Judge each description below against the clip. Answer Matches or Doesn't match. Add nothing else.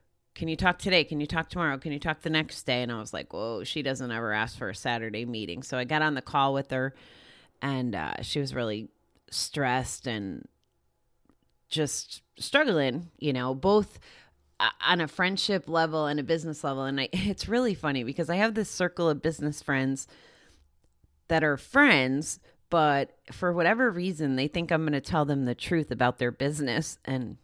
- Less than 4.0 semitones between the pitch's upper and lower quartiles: Doesn't match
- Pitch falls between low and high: Matches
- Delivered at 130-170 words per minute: Doesn't match